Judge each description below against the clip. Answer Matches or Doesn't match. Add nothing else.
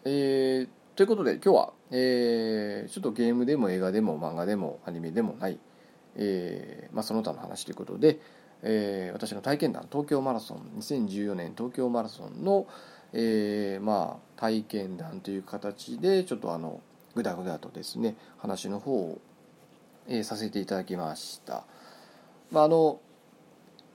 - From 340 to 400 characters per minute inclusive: Doesn't match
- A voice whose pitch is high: Doesn't match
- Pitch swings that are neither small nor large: Matches